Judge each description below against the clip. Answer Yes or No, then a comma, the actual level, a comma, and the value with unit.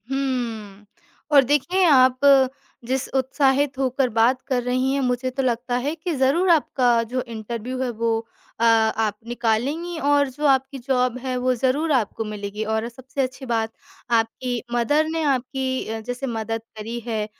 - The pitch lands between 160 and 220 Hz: No, very high, 255 Hz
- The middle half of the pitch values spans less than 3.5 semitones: Yes, average, 2.8 semitones